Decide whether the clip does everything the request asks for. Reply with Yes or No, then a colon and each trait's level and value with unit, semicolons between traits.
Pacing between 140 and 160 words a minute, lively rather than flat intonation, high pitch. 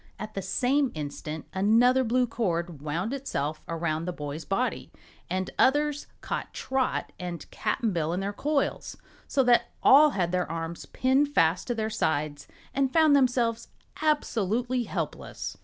Yes: average, 150 wpm; wide, 7.5 semitones; high, 215 Hz